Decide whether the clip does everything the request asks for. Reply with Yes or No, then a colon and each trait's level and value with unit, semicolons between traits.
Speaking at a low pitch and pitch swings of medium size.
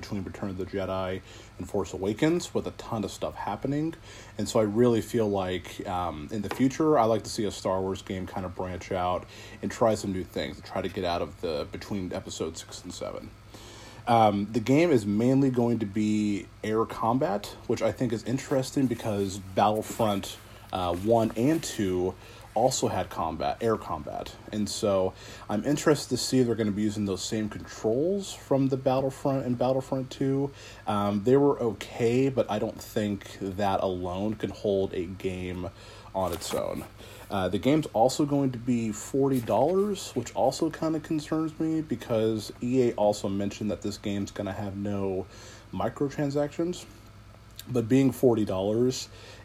Yes: low, 110 Hz; average, 4.2 semitones